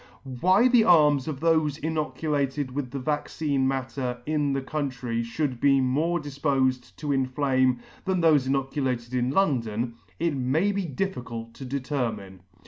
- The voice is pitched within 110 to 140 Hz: Yes, low, 135 Hz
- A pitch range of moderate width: Yes, average, 3.2 semitones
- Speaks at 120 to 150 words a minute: Yes, average, 140 wpm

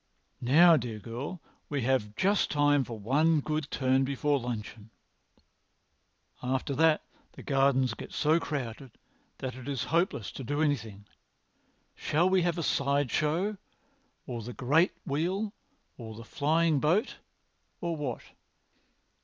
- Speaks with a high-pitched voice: No, medium, 140 Hz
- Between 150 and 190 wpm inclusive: No, slow, 135 wpm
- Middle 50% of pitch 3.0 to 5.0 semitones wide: Yes, average, 4.4 semitones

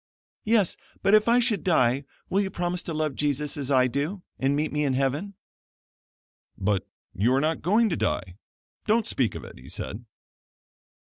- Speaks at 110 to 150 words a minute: No, average, 180 wpm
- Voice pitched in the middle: Yes, medium, 150 Hz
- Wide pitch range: Yes, wide, 6.9 semitones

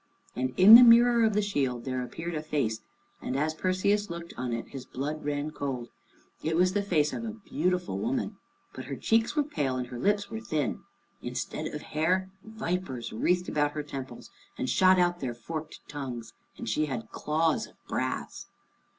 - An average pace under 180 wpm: No, average, 185 wpm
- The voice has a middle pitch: Yes, medium, 155 Hz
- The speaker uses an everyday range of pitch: No, wide, 6.5 semitones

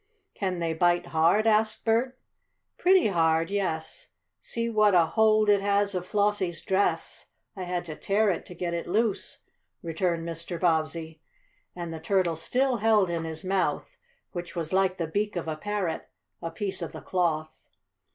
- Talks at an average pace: Yes, average, 170 wpm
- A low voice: No, medium, 180 Hz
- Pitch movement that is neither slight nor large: Yes, average, 3.8 semitones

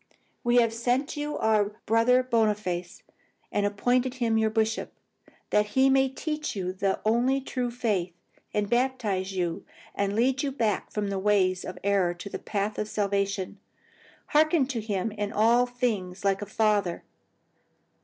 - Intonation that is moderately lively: Yes, average, 3.8 semitones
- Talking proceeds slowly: No, average, 160 wpm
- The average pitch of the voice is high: Yes, high, 215 Hz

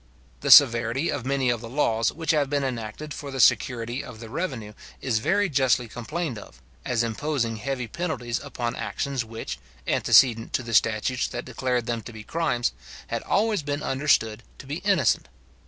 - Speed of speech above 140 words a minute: Yes, average, 175 wpm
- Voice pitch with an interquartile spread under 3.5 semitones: No, average, 3.9 semitones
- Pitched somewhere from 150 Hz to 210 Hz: No, low, 125 Hz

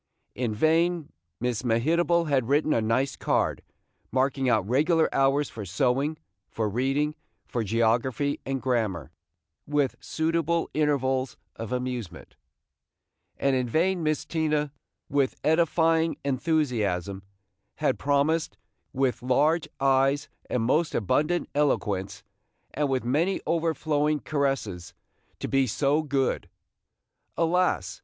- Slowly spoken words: Yes, slow, 115 wpm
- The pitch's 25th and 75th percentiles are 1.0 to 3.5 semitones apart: No, average, 4.0 semitones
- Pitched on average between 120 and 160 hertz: Yes, medium, 140 Hz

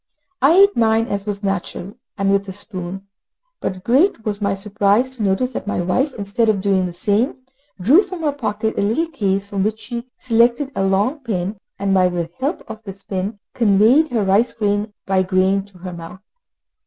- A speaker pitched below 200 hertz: No, high, 205 Hz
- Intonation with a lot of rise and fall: No, average, 3.4 semitones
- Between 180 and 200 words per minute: Yes, average, 190 wpm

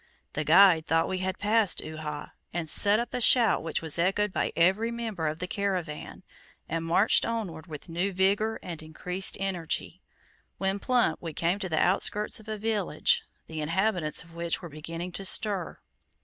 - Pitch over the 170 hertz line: Yes, medium, 185 Hz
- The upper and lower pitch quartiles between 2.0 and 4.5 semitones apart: Yes, average, 3.9 semitones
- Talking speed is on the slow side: No, average, 175 wpm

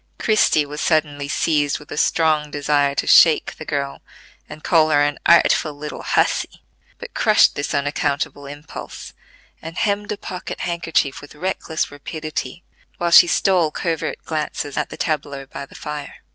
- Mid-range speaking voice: Yes, medium, 150 Hz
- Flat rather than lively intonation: Yes, narrow, 2.2 semitones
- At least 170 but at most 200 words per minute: No, average, 160 wpm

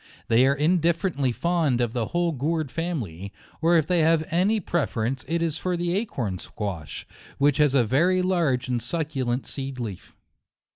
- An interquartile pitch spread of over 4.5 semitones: Yes, wide, 5.6 semitones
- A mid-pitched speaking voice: Yes, medium, 145 Hz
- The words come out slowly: No, average, 175 wpm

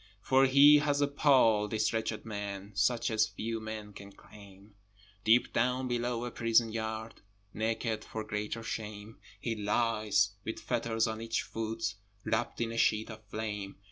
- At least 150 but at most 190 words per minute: Yes, average, 160 wpm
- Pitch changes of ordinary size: No, narrow, 1.5 semitones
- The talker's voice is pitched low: Yes, low, 110 Hz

